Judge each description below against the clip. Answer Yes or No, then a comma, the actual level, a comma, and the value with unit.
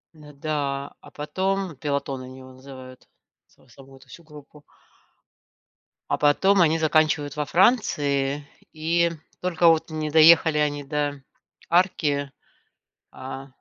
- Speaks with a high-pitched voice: No, medium, 150 Hz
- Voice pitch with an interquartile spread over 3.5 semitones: No, average, 2.7 semitones